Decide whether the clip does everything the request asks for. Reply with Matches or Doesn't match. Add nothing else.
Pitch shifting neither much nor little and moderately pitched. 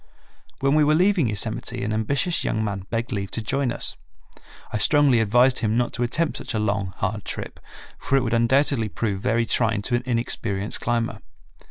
Doesn't match